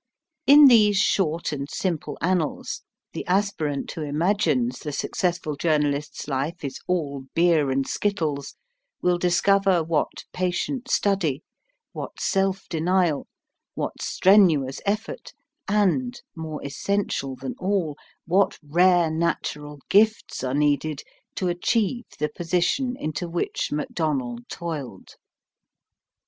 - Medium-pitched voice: Yes, medium, 170 Hz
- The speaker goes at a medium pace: No, slow, 110 wpm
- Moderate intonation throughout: Yes, average, 4.6 semitones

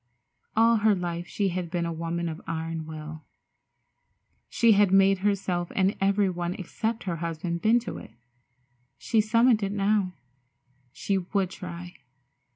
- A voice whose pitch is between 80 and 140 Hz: No, medium, 185 Hz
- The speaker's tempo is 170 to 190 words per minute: No, average, 150 wpm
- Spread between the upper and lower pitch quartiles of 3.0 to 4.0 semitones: Yes, average, 3.3 semitones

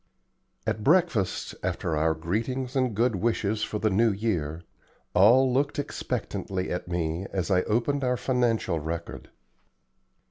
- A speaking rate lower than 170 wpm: Yes, slow, 135 wpm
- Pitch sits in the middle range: No, low, 105 Hz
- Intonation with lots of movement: Yes, wide, 5.9 semitones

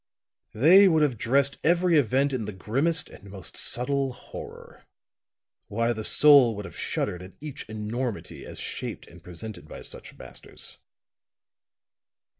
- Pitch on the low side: Yes, low, 125 Hz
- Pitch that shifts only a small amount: No, average, 5.2 semitones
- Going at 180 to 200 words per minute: No, average, 140 wpm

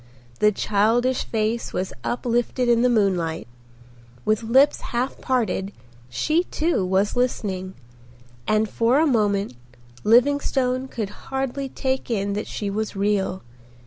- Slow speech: Yes, slow, 125 wpm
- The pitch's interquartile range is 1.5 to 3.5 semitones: No, average, 4.1 semitones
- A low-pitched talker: No, high, 225 Hz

